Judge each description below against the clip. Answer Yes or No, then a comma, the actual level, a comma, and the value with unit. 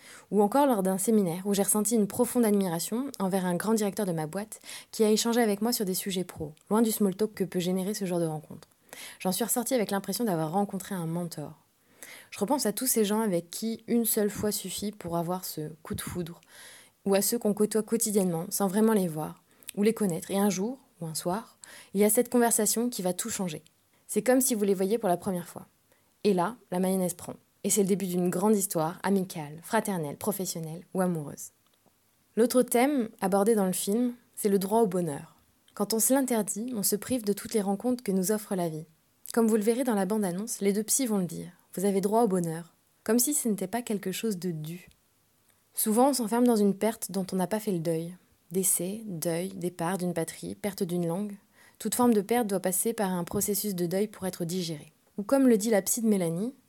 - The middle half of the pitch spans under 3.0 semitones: No, average, 3.7 semitones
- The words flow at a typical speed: No, fast, 230 wpm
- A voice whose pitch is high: Yes, high, 200 Hz